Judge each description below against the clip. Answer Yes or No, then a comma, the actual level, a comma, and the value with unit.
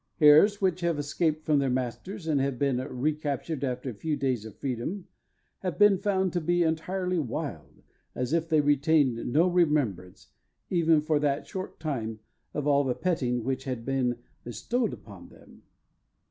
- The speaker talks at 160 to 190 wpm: Yes, average, 165 wpm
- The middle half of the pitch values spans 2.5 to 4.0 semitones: No, average, 4.7 semitones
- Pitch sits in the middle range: Yes, medium, 150 Hz